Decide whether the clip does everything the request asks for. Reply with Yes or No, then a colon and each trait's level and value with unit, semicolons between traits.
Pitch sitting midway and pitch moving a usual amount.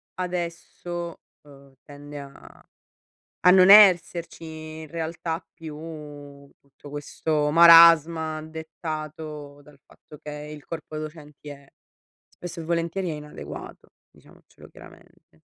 No: medium, 155 Hz; narrow, 2.1 semitones